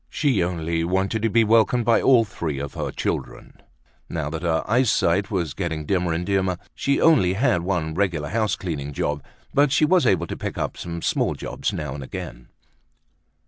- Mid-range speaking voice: No, very low, 90 Hz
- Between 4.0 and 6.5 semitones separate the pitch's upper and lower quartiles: Yes, wide, 5.6 semitones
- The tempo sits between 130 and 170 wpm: No, average, 185 wpm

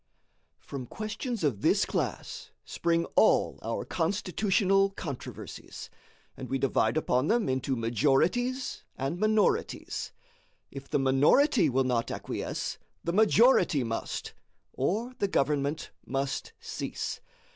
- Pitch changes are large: Yes, wide, 7.8 semitones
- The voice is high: No, medium, 160 Hz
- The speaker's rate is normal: No, slow, 115 wpm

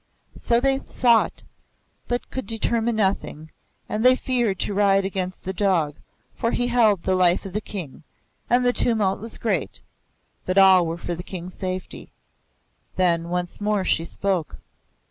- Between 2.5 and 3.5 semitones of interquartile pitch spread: No, average, 4.1 semitones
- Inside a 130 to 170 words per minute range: Yes, average, 160 wpm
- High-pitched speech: Yes, high, 195 Hz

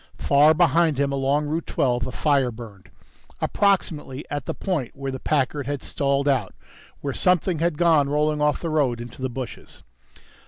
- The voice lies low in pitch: No, medium, 145 Hz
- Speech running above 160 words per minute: Yes, average, 170 wpm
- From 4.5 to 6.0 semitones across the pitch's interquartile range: No, average, 2.8 semitones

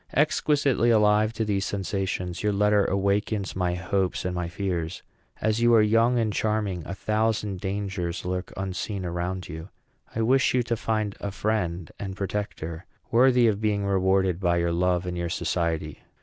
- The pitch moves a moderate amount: Yes, average, 3.2 semitones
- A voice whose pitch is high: No, low, 100 Hz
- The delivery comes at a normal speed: Yes, average, 165 wpm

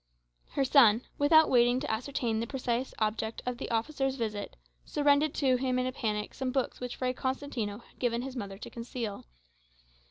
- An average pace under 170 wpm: No, average, 180 wpm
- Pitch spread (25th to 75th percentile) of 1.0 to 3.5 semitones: Yes, average, 2.9 semitones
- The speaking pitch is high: Yes, very high, 250 Hz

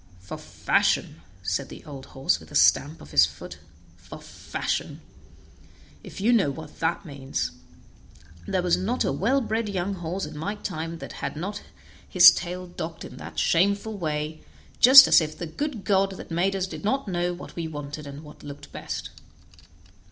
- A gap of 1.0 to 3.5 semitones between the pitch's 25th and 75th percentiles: No, average, 4.8 semitones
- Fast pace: No, average, 180 wpm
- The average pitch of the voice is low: No, medium, 175 Hz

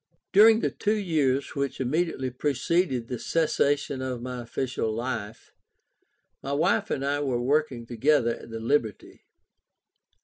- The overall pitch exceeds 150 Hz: No, low, 135 Hz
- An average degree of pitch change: Yes, average, 4.0 semitones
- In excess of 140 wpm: No, slow, 135 wpm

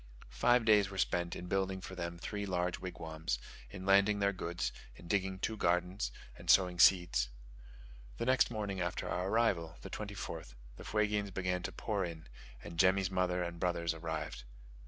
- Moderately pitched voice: No, very low, 90 Hz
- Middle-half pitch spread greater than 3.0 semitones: No, narrow, 2.5 semitones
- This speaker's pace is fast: No, average, 170 wpm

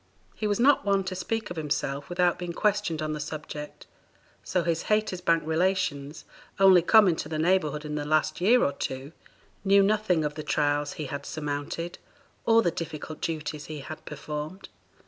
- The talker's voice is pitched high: No, medium, 160 Hz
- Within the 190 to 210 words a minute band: No, average, 175 wpm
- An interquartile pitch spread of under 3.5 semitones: No, average, 4.1 semitones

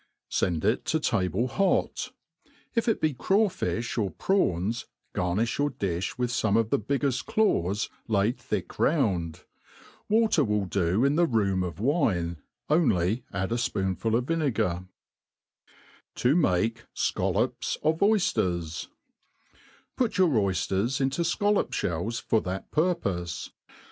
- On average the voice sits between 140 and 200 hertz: No, low, 115 Hz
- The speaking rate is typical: No, slow, 120 wpm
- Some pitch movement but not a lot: No, wide, 8.3 semitones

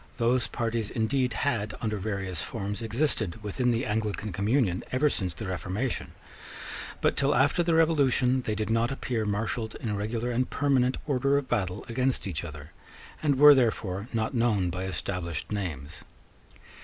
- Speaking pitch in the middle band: No, low, 115 Hz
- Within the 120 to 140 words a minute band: No, average, 155 wpm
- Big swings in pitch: No, average, 4.4 semitones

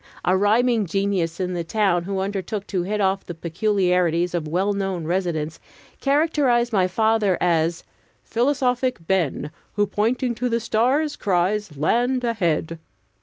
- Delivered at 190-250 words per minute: No, average, 140 wpm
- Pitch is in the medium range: No, high, 195 Hz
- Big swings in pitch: No, average, 4.8 semitones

